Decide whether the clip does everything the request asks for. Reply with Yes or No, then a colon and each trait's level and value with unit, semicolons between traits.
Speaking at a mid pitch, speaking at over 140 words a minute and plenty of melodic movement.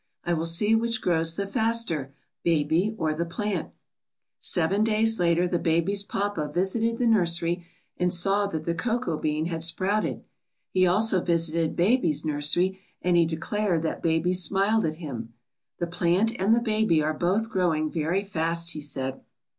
No: medium, 175 Hz; average, 160 wpm; average, 4.0 semitones